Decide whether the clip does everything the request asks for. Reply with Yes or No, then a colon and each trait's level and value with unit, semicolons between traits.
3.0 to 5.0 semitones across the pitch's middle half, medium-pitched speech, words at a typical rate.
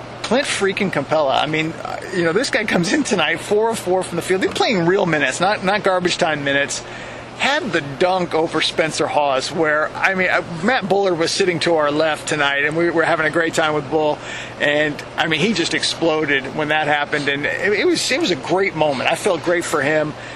No: average, 3.5 semitones; medium, 160 Hz; fast, 220 wpm